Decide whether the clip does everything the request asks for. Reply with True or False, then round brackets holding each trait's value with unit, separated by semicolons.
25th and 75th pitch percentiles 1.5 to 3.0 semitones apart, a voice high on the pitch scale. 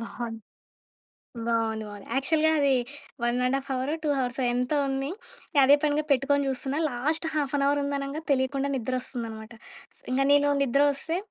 True (2.6 semitones; 270 Hz)